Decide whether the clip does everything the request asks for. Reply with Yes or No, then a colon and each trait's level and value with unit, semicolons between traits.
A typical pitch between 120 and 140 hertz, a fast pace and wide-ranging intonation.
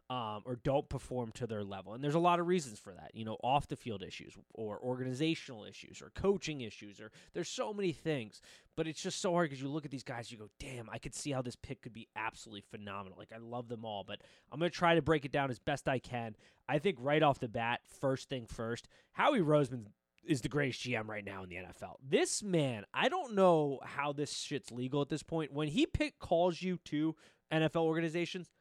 Yes: low, 135 Hz; fast, 235 wpm; wide, 5.9 semitones